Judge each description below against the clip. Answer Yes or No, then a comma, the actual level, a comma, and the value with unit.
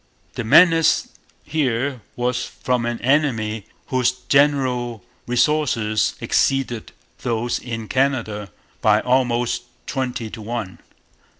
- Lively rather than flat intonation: No, average, 2.7 semitones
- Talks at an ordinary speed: No, slow, 100 wpm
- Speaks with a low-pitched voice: Yes, low, 125 Hz